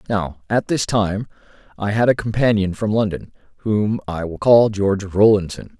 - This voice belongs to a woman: No, male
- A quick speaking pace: No, average, 165 wpm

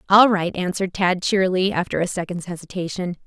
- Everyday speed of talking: Yes, average, 165 wpm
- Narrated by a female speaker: Yes, female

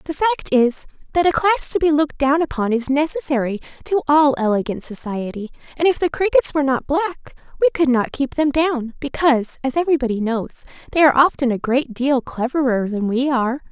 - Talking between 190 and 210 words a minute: Yes, average, 195 wpm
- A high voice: Yes, very high, 275 Hz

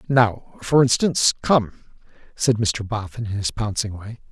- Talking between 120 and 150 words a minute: Yes, average, 140 wpm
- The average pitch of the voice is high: No, low, 110 Hz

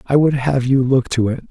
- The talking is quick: Yes, fast, 280 wpm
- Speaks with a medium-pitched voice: No, low, 130 Hz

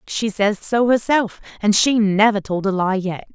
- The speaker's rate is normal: Yes, average, 180 wpm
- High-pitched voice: Yes, high, 210 Hz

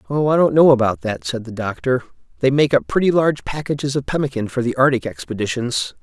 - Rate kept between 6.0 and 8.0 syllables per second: Yes, 6.1 syllables/s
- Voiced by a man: Yes, male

